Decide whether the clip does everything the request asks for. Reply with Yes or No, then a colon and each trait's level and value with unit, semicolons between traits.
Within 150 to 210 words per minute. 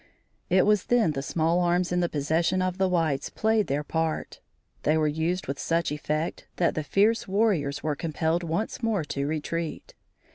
Yes: average, 180 wpm